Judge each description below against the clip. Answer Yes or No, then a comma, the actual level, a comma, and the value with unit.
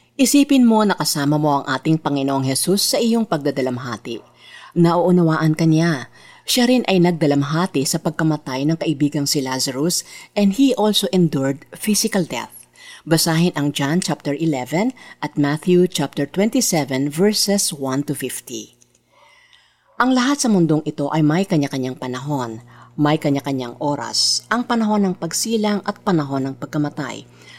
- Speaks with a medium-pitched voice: Yes, medium, 155 Hz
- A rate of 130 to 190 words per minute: Yes, average, 140 wpm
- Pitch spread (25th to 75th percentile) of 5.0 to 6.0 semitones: Yes, average, 5.3 semitones